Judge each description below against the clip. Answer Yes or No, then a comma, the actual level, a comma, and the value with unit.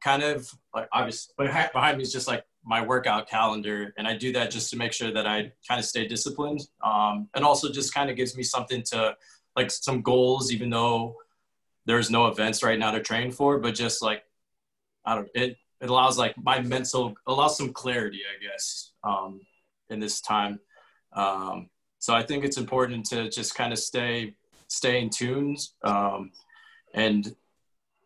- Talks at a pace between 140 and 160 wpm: No, average, 185 wpm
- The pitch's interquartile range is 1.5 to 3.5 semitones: Yes, average, 2.9 semitones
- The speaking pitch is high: No, low, 120 Hz